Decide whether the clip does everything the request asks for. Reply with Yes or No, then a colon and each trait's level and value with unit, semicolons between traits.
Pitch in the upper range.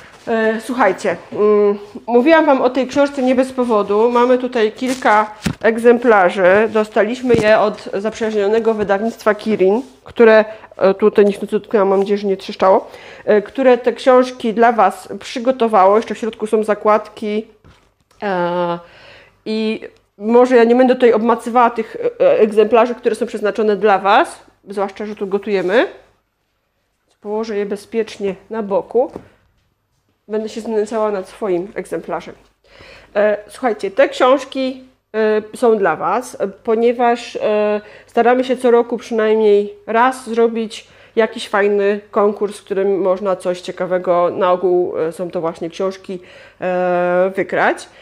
Yes: high, 215 Hz